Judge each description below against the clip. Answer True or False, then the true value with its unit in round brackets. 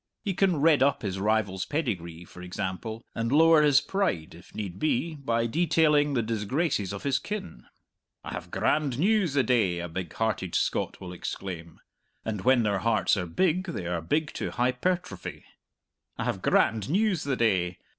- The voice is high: False (115 Hz)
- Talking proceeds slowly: False (175 wpm)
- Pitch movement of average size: False (8.5 semitones)